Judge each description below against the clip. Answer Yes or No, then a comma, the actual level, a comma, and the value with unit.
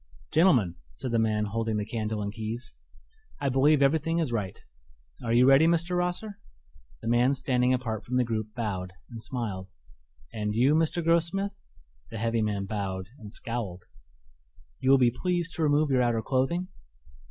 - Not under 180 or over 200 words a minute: No, average, 165 wpm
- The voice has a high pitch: No, low, 120 Hz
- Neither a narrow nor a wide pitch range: No, wide, 5.8 semitones